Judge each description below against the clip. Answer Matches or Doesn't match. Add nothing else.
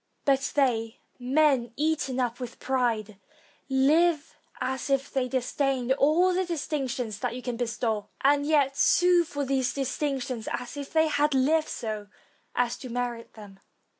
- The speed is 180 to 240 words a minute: Doesn't match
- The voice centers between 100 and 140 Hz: Doesn't match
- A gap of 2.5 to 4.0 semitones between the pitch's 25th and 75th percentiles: Matches